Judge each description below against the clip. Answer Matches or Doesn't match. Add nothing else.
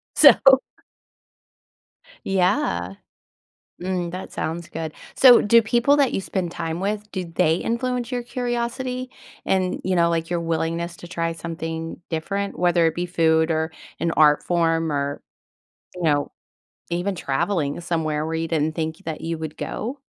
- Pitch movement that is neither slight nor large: Matches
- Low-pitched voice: Doesn't match